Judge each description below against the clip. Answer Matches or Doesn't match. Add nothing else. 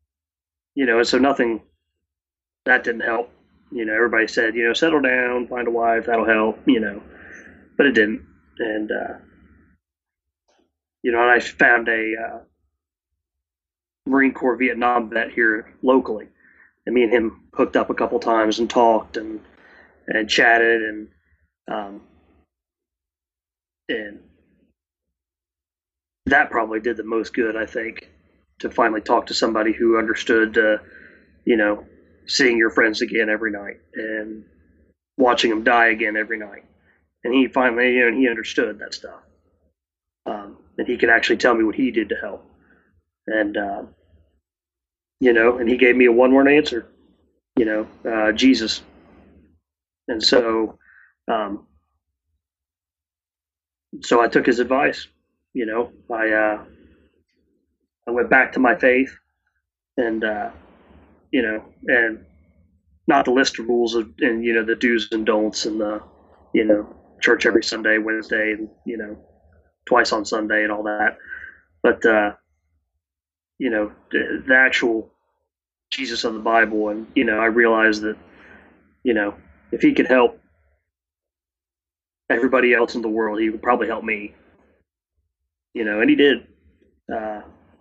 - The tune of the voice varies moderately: Doesn't match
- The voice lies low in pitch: Matches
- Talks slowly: Doesn't match